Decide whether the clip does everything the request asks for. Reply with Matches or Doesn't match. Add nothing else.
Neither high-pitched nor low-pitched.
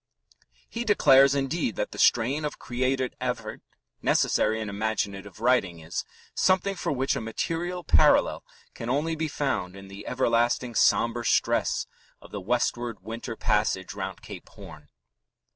Doesn't match